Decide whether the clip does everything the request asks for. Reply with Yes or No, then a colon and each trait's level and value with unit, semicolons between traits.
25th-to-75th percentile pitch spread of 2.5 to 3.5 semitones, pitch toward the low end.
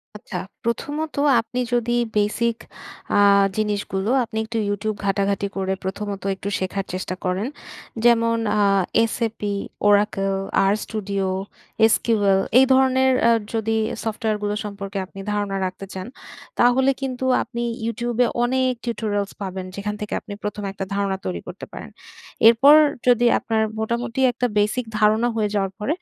No: average, 3.0 semitones; high, 210 Hz